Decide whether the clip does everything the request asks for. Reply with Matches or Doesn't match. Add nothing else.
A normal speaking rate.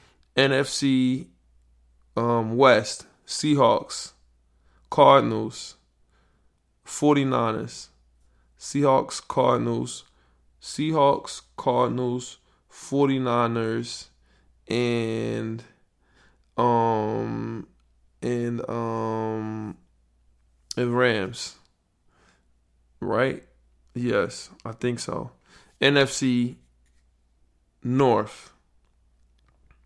Doesn't match